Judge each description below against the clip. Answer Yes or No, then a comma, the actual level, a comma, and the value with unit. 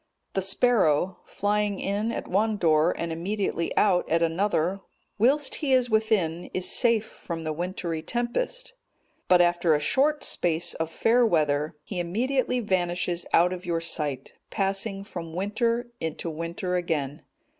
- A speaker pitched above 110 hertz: Yes, medium, 185 Hz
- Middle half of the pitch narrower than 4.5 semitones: No, average, 4.8 semitones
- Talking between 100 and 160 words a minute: Yes, average, 145 wpm